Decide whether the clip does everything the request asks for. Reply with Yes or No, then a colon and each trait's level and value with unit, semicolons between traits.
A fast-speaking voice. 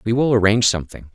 Yes: fast, 210 wpm